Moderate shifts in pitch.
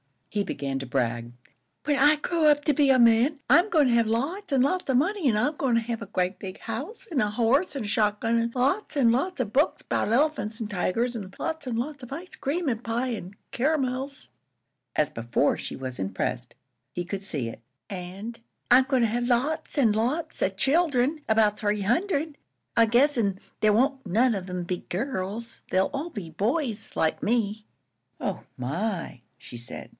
No: wide, 5.8 semitones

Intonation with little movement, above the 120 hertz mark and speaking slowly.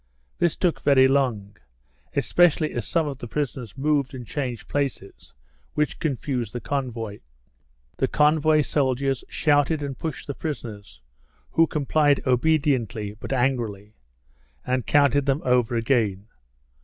No: average, 3.7 semitones; low, 135 Hz; slow, 130 wpm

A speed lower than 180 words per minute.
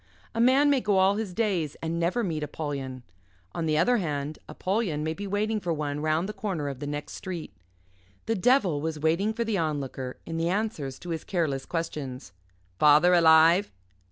No: average, 185 wpm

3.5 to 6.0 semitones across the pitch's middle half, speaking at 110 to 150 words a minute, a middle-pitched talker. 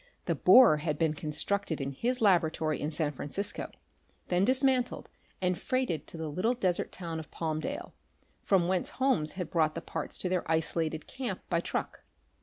No: average, 4.4 semitones; average, 170 wpm; medium, 170 Hz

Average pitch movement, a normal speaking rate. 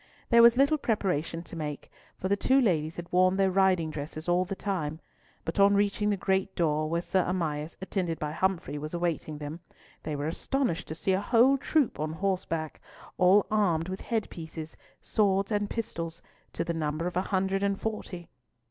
Yes: average, 3.8 semitones; average, 190 wpm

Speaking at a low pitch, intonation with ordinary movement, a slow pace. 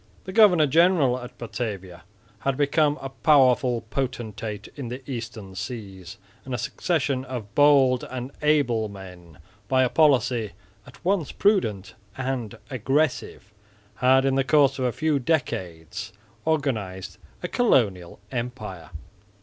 Yes: low, 125 Hz; average, 5.0 semitones; slow, 130 wpm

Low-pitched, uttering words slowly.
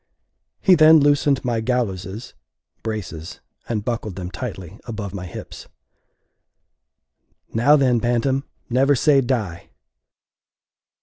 Yes: low, 120 Hz; slow, 105 wpm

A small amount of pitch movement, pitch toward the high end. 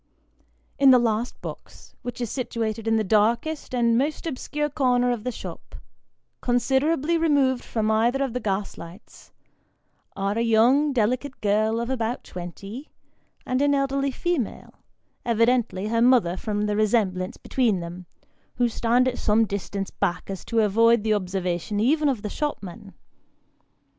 No: average, 3.7 semitones; high, 230 Hz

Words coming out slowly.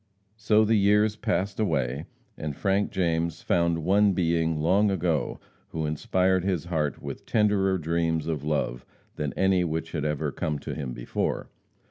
No: average, 155 wpm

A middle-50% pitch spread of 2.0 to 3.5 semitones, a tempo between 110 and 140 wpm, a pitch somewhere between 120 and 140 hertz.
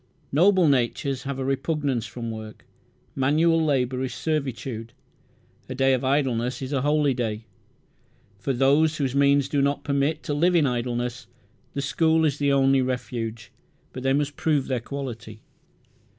No: average, 2.9 semitones; average, 155 wpm; low, 135 Hz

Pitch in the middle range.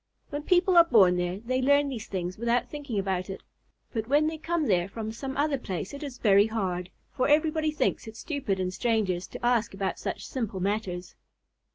No: high, 225 Hz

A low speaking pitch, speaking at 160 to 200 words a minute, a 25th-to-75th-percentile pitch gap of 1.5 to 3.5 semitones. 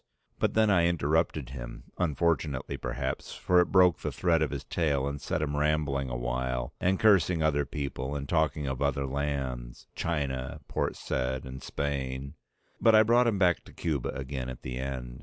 No: very low, 70 Hz; average, 180 wpm; average, 4.0 semitones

